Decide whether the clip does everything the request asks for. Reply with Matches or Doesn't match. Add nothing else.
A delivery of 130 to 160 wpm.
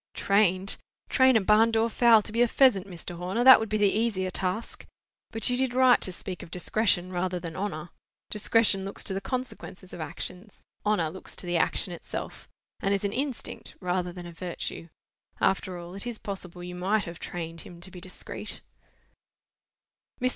Doesn't match